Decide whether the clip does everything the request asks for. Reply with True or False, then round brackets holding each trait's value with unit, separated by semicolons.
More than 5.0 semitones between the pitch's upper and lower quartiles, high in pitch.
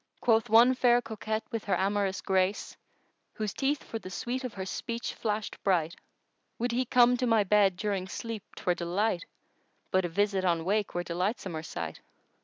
False (3.6 semitones; 205 Hz)